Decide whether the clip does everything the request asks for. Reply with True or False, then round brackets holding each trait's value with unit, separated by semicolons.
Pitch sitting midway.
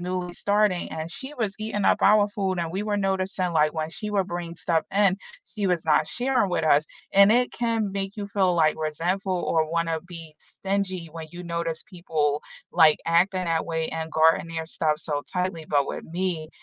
True (175 Hz)